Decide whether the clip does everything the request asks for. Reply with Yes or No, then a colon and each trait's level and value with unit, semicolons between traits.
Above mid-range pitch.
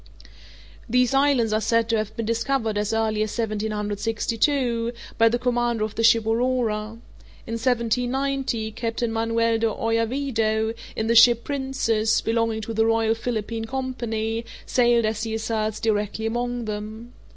Yes: high, 225 Hz